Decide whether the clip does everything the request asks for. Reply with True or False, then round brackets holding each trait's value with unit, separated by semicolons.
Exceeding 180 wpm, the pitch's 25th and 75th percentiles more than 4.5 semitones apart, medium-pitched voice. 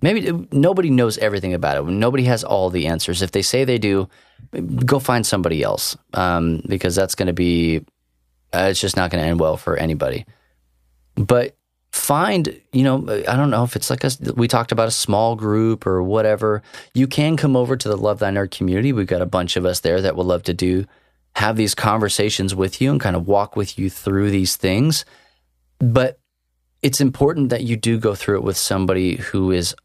False (200 wpm; 4.9 semitones; 100 Hz)